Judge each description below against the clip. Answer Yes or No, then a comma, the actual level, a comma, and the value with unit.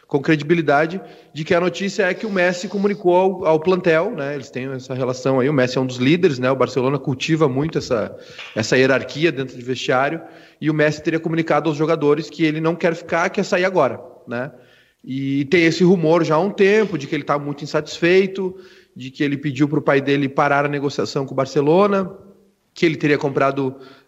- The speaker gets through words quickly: Yes, fast, 210 wpm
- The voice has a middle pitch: Yes, medium, 155 Hz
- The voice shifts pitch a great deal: No, average, 4.4 semitones